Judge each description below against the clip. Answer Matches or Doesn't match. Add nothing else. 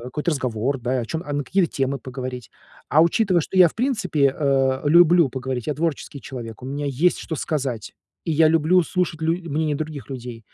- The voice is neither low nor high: Matches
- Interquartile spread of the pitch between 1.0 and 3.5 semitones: Doesn't match